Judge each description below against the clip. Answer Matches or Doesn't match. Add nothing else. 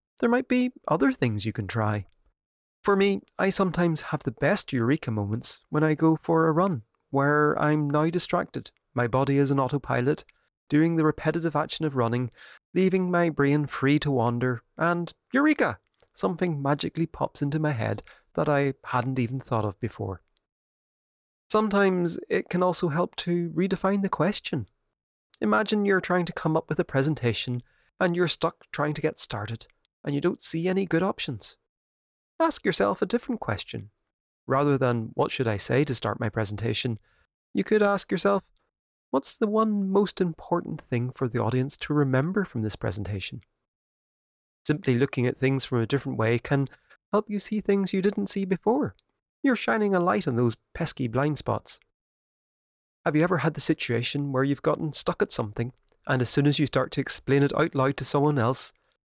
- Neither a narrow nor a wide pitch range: Doesn't match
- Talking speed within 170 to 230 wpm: Matches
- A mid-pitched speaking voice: Matches